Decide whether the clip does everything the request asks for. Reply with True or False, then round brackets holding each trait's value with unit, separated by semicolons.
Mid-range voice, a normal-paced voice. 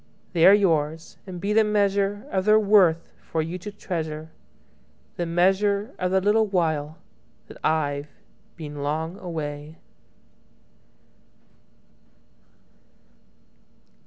False (175 Hz; 95 wpm)